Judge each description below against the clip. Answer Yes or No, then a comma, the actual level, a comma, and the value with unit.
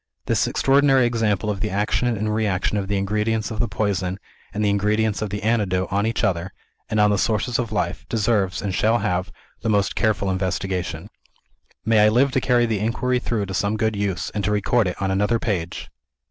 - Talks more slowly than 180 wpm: No, fast, 205 wpm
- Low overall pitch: Yes, low, 105 Hz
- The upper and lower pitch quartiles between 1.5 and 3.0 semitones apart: Yes, narrow, 2.5 semitones